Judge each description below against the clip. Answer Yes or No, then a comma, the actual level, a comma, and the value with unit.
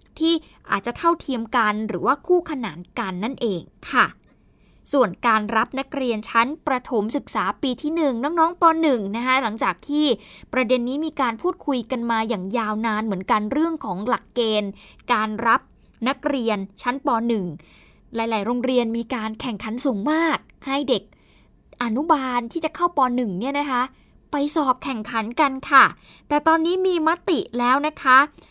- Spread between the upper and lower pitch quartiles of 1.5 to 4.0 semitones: No, average, 4.4 semitones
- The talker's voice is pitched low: No, very high, 255 Hz